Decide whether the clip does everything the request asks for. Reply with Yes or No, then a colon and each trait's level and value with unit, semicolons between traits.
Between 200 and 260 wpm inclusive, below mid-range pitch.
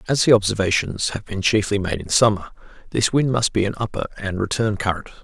Yes: fast, 205 wpm; low, 105 Hz